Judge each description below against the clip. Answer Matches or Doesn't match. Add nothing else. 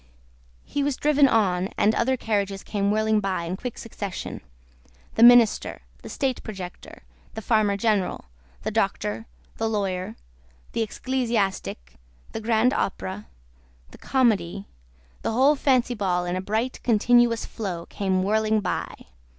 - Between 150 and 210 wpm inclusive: Doesn't match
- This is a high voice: Matches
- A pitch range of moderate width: Matches